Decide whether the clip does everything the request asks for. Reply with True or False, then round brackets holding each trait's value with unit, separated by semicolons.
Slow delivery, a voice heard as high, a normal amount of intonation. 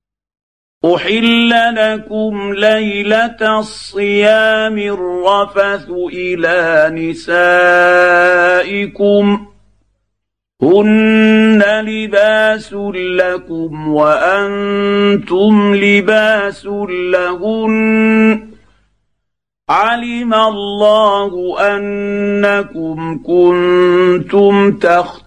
True (45 wpm; 200 Hz; 3.3 semitones)